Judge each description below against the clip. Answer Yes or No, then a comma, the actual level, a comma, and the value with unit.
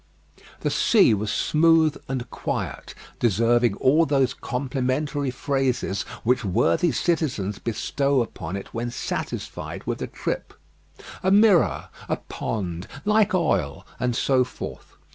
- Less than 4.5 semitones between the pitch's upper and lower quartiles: No, average, 4.8 semitones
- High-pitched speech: No, low, 130 Hz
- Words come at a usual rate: No, slow, 125 wpm